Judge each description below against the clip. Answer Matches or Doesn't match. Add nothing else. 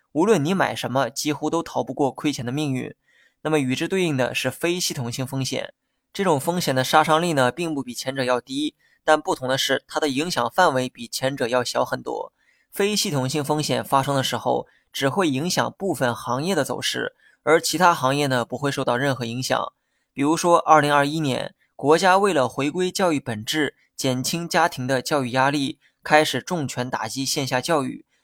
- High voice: Doesn't match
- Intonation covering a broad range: Doesn't match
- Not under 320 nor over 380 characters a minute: Doesn't match